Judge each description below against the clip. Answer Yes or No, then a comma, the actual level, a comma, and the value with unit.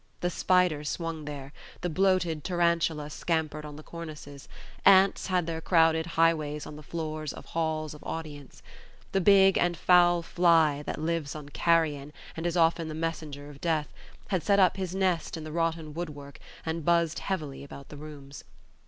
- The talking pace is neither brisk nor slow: Yes, average, 170 wpm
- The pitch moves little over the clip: Yes, narrow, 2.3 semitones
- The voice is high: No, medium, 160 Hz